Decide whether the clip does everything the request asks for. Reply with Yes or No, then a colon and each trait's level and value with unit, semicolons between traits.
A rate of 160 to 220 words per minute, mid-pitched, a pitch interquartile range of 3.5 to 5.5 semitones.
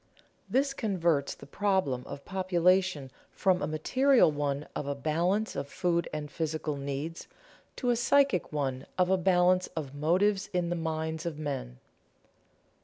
No: average, 150 wpm; medium, 170 Hz; average, 4.4 semitones